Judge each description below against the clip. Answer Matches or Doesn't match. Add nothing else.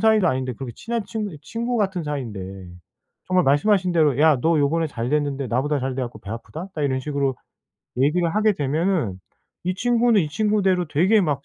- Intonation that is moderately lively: Doesn't match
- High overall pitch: Doesn't match